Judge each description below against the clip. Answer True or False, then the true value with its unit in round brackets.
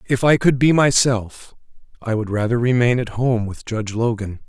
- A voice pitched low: True (120 Hz)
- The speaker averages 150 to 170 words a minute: False (190 wpm)